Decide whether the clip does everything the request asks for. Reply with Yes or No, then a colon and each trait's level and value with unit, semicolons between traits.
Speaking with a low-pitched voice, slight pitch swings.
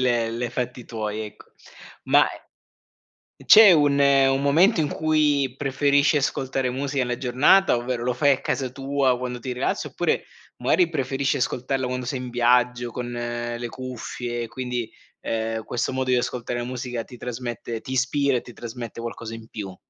Yes: low, 125 Hz; narrow, 2.2 semitones